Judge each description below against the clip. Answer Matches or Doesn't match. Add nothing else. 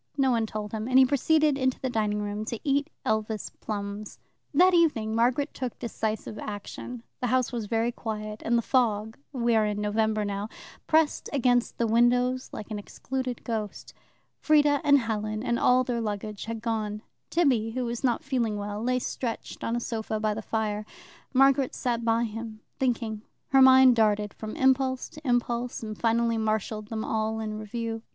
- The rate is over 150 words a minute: Matches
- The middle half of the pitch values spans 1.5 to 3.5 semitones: Matches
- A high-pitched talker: Matches